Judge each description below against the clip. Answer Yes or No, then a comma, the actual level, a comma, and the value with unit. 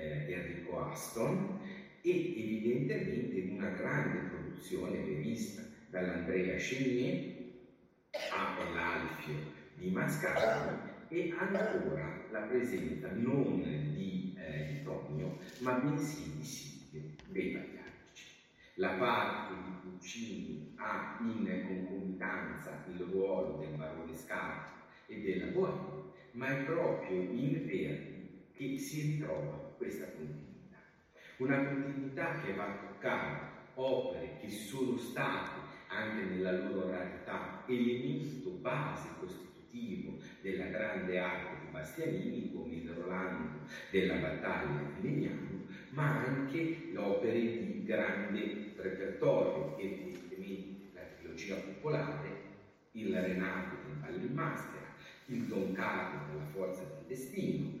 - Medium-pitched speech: No, very low, 95 Hz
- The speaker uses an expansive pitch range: Yes, wide, 6.8 semitones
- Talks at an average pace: No, slow, 110 wpm